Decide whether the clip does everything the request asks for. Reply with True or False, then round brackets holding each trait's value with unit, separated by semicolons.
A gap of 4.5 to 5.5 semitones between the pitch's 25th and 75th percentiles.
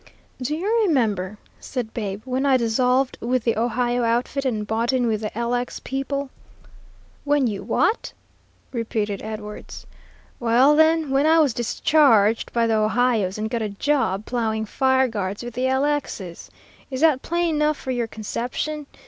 False (4.0 semitones)